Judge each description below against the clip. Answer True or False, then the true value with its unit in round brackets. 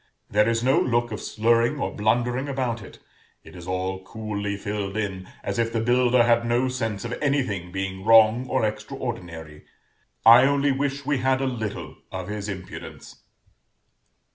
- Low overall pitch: True (115 Hz)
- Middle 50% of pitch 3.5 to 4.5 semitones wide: True (4.0 semitones)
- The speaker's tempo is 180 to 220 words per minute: False (165 wpm)